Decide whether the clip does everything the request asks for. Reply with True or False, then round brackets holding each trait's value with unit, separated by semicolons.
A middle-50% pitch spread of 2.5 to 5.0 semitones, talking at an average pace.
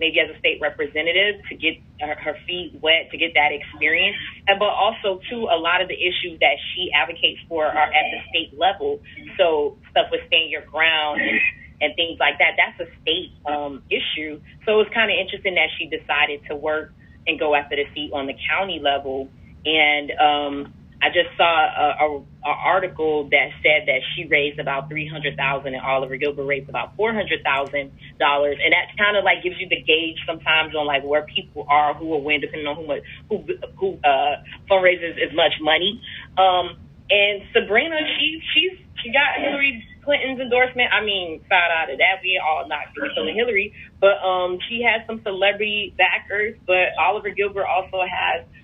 False (5.5 semitones; 190 wpm)